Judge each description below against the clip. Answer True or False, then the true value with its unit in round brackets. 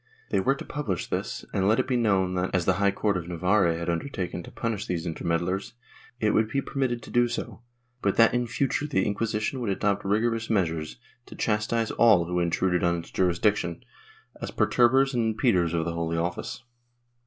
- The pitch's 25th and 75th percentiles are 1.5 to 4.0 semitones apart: False (4.8 semitones)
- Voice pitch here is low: True (100 Hz)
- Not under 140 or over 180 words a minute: False (195 wpm)